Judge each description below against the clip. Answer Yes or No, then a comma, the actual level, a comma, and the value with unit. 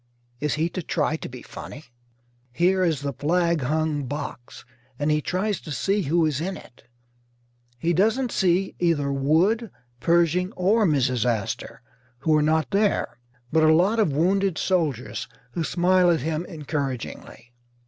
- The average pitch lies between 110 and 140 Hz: No, medium, 160 Hz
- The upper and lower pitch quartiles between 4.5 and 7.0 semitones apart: No, average, 4.1 semitones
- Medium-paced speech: Yes, average, 155 wpm